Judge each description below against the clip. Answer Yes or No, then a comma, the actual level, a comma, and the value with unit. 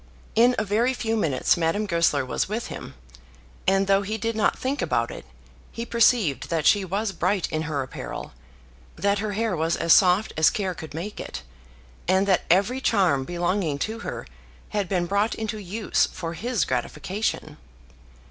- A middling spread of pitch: Yes, average, 4.5 semitones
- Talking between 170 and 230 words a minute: Yes, average, 175 wpm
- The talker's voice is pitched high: Yes, high, 195 Hz